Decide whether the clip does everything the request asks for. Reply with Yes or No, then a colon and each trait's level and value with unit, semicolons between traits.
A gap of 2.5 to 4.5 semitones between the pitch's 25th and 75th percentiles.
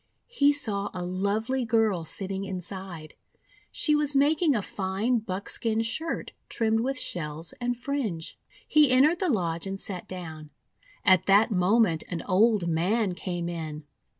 No: wide, 5.4 semitones